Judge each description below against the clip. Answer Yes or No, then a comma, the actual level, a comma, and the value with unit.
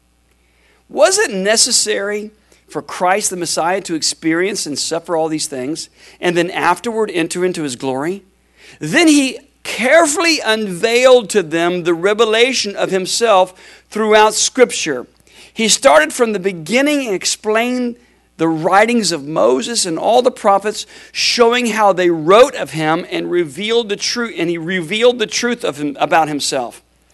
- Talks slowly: No, average, 150 wpm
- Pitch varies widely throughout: Yes, wide, 5.8 semitones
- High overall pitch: Yes, high, 200 Hz